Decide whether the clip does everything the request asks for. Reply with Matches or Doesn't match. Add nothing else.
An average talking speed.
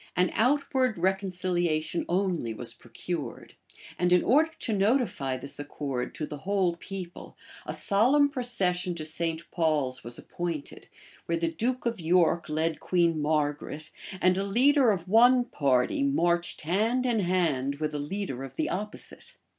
Matches